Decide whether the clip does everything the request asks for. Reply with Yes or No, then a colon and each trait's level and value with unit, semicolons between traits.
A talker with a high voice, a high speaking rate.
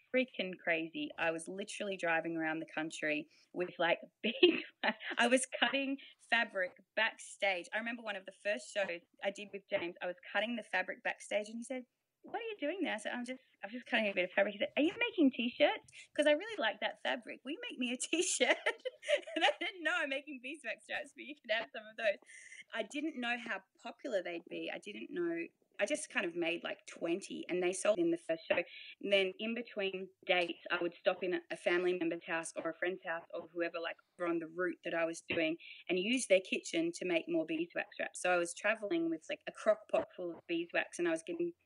Yes: very high, 250 Hz; fast, 235 wpm